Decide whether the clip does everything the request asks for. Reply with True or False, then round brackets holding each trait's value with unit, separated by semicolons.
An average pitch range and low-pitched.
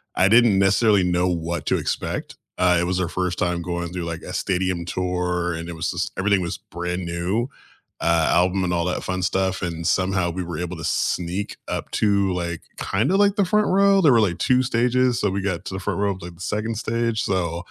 True (3.0 semitones; 90 Hz)